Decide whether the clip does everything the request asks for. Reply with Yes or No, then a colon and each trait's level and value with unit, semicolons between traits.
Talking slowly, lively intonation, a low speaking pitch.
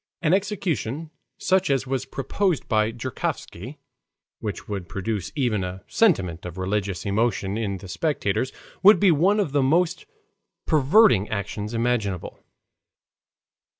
Yes: slow, 125 wpm; wide, 8.0 semitones; low, 120 Hz